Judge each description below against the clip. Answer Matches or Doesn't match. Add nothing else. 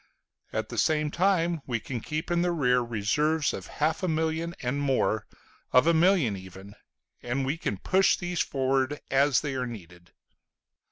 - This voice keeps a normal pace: Matches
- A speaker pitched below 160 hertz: Matches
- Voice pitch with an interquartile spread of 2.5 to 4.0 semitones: Doesn't match